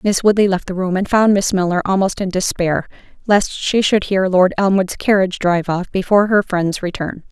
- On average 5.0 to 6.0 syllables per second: Yes, 5.4 syllables/s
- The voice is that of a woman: Yes, female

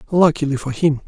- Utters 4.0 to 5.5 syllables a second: No, 6.0 syllables/s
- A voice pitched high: No, medium, 145 Hz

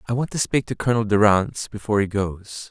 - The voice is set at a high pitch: No, low, 110 Hz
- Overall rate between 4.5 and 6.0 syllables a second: No, 6.2 syllables/s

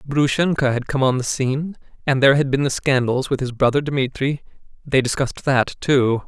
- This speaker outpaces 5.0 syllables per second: Yes, 5.5 syllables/s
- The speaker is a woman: No, male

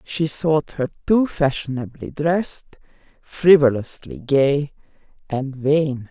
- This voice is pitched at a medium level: Yes, medium, 145 Hz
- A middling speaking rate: No, slow, 100 wpm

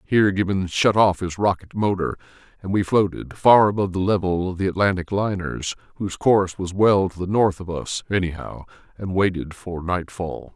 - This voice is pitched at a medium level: No, very low, 95 Hz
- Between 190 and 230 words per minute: No, average, 180 wpm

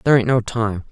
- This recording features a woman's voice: No, male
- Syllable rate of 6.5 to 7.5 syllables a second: Yes, 6.7 syllables/s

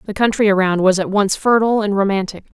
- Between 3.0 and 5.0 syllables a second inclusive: No, 6.3 syllables/s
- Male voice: No, female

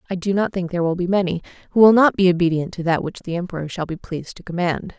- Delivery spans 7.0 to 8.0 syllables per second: Yes, 7.1 syllables/s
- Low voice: No, medium, 180 Hz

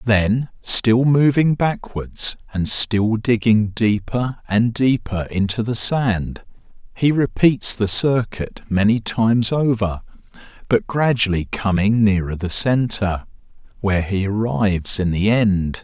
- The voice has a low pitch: Yes, low, 110 Hz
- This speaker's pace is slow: Yes, slow, 120 wpm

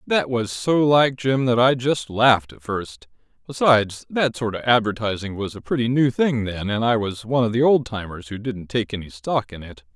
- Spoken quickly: Yes, fast, 225 wpm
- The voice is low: Yes, low, 115 Hz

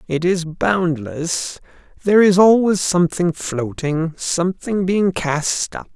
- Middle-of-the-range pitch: Yes, medium, 175 Hz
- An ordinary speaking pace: No, slow, 120 wpm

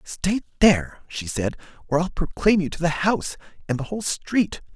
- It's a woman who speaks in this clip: No, male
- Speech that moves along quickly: No, average, 190 wpm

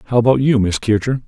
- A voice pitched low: Yes, low, 120 Hz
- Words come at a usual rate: No, fast, 235 wpm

